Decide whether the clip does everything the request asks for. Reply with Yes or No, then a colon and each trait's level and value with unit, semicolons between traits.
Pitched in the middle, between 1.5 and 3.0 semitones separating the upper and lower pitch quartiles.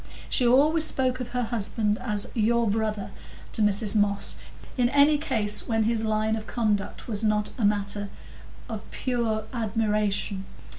No: high, 220 Hz; narrow, 2.5 semitones